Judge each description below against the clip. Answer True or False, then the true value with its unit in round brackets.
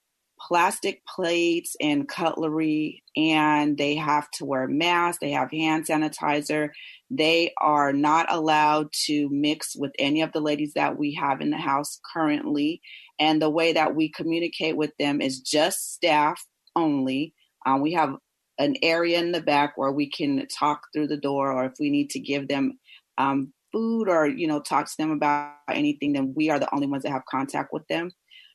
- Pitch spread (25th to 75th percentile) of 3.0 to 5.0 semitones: False (2.4 semitones)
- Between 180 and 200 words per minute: True (185 wpm)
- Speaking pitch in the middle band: True (150 Hz)